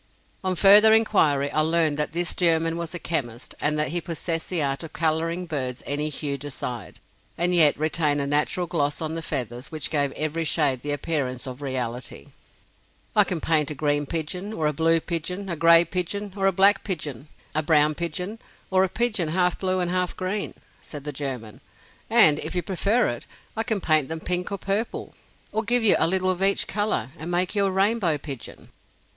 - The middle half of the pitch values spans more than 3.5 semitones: Yes, average, 3.9 semitones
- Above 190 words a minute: Yes, average, 200 wpm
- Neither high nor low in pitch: Yes, medium, 165 Hz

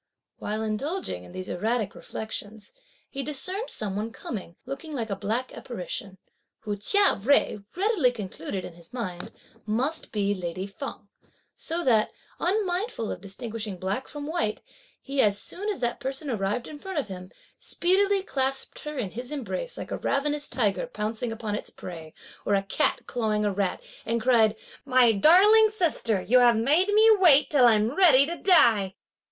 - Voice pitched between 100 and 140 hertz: No, high, 240 Hz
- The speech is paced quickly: No, average, 170 wpm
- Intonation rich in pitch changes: Yes, wide, 6.5 semitones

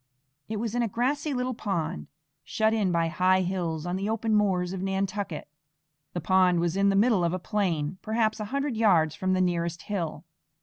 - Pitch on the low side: No, high, 190 Hz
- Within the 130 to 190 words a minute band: No, average, 200 wpm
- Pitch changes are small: No, average, 3.7 semitones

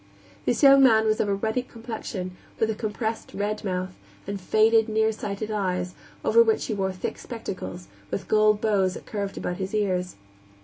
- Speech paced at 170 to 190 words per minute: Yes, average, 175 wpm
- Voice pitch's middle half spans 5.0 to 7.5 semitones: No, narrow, 2.6 semitones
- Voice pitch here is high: Yes, high, 210 Hz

